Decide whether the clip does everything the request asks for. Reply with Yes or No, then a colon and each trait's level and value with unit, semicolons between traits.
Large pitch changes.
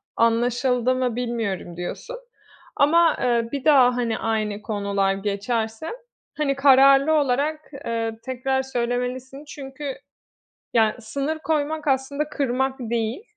No: average, 3.5 semitones